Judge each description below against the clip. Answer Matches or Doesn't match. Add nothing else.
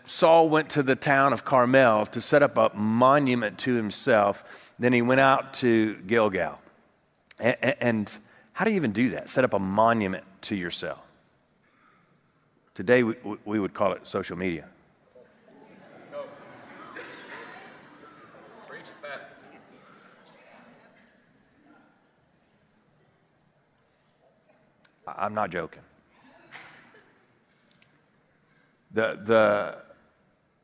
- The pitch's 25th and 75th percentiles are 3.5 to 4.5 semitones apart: Matches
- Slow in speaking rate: Matches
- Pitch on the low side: Matches